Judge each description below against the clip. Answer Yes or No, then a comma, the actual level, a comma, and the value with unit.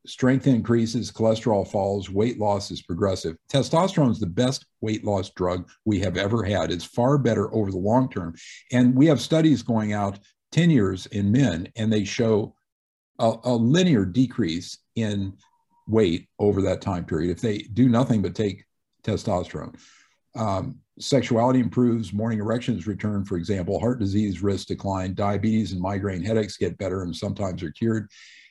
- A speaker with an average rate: Yes, average, 165 wpm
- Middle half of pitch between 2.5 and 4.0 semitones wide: Yes, average, 3.4 semitones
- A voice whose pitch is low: Yes, low, 105 Hz